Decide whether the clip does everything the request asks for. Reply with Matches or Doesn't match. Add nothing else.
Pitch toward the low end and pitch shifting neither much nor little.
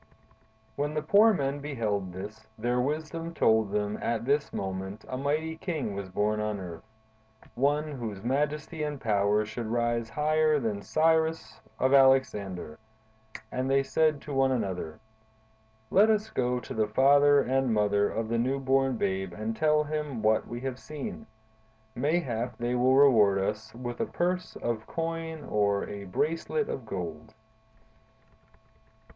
Doesn't match